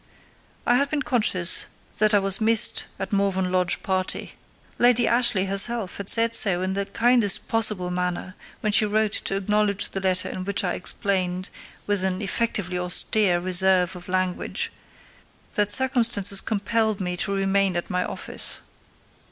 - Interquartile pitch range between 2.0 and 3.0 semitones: Yes, average, 2.7 semitones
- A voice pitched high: Yes, high, 195 Hz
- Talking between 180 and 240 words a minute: No, average, 155 wpm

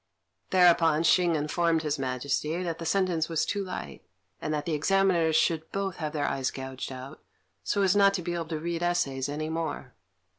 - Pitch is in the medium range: Yes, medium, 160 Hz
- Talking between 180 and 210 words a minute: Yes, average, 190 wpm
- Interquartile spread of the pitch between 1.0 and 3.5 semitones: Yes, average, 2.9 semitones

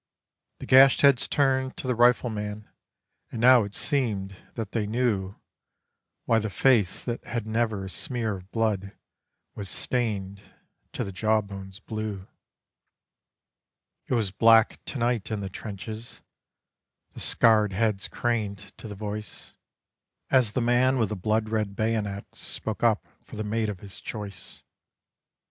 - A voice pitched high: No, low, 110 Hz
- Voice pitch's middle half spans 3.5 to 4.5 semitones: No, average, 2.8 semitones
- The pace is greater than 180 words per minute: No, average, 145 wpm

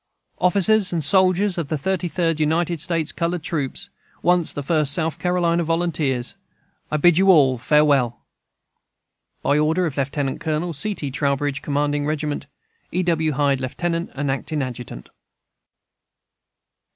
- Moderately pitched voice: Yes, medium, 155 Hz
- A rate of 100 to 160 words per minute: Yes, average, 140 wpm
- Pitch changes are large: No, average, 3.5 semitones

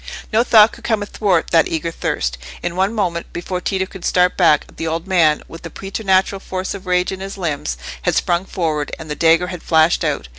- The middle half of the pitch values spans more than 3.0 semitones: No, average, 2.7 semitones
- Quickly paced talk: Yes, fast, 215 wpm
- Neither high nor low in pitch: Yes, medium, 180 Hz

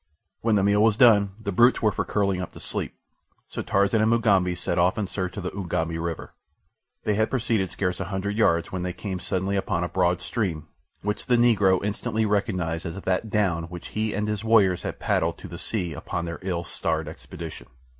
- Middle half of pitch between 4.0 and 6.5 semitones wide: No, average, 3.1 semitones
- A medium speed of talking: No, fast, 210 wpm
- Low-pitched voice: Yes, very low, 95 Hz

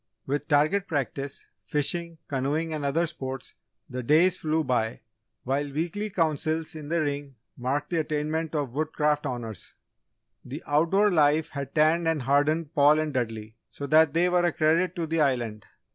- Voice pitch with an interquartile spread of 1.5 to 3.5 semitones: Yes, average, 2.7 semitones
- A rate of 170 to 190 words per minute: No, average, 160 wpm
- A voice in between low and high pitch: Yes, medium, 150 Hz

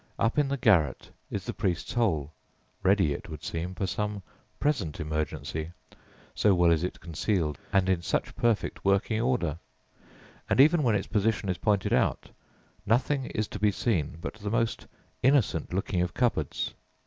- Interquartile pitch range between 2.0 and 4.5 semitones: No, average, 5.2 semitones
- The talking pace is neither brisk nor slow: Yes, average, 165 wpm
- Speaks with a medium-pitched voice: No, low, 100 Hz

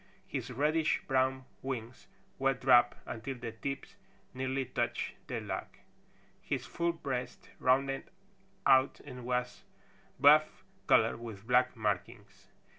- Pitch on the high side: No, low, 130 Hz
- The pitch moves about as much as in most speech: No, narrow, 2.1 semitones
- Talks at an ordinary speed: No, slow, 115 wpm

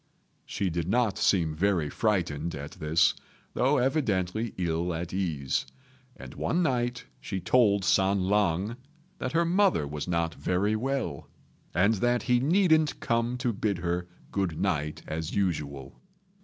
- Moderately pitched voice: No, very low, 95 Hz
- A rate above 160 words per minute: No, average, 140 wpm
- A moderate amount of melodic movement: No, wide, 6.4 semitones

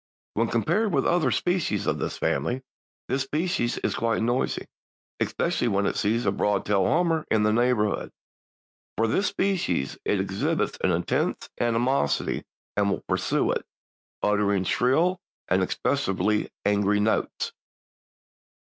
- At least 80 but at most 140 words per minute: Yes, slow, 135 wpm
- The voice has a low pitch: Yes, low, 115 Hz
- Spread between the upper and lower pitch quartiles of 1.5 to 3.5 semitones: No, wide, 5.5 semitones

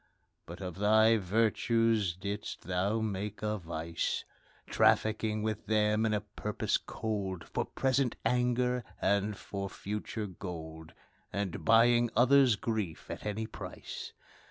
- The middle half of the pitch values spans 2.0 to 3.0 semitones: Yes, average, 2.7 semitones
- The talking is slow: Yes, slow, 125 wpm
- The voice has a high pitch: No, low, 105 Hz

